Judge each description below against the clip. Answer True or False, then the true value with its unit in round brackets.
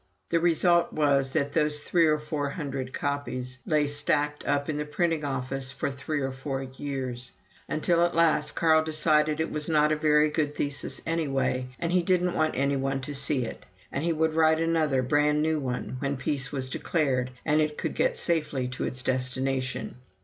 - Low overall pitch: False (150 Hz)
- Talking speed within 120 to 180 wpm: False (190 wpm)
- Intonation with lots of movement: False (2.7 semitones)